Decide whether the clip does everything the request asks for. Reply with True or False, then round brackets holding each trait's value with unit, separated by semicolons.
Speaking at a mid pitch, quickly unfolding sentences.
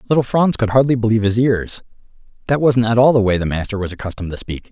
False (115 Hz; 240 wpm)